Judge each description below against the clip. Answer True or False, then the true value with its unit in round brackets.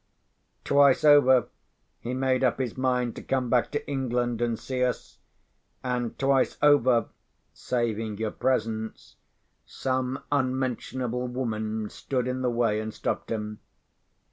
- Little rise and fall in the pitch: True (2.3 semitones)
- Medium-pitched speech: False (125 Hz)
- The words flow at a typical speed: False (130 wpm)